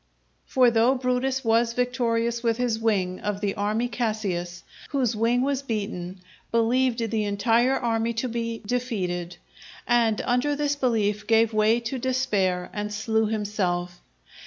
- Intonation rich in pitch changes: No, average, 3.0 semitones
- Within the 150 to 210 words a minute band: No, average, 140 wpm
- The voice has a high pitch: Yes, high, 230 Hz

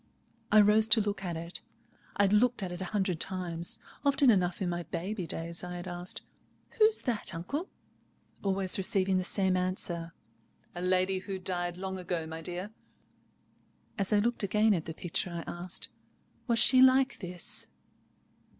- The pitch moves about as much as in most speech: Yes, average, 3.0 semitones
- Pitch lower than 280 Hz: Yes, medium, 185 Hz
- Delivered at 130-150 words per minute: No, average, 170 wpm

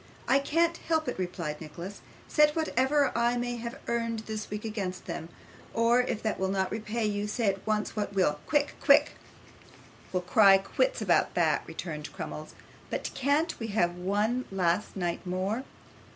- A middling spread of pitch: Yes, average, 4.6 semitones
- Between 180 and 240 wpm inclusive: No, average, 165 wpm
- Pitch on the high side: Yes, high, 215 Hz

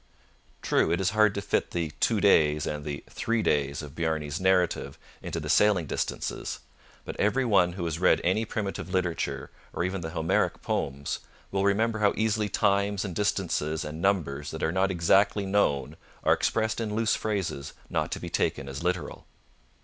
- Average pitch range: Yes, average, 4.5 semitones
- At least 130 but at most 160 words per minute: No, average, 180 wpm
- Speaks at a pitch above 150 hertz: No, very low, 95 Hz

